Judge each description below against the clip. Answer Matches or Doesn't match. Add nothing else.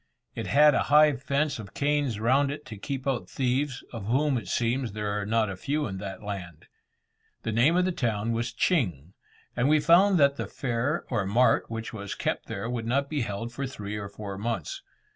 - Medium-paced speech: Doesn't match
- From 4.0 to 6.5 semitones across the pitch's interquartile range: Matches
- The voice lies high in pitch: Doesn't match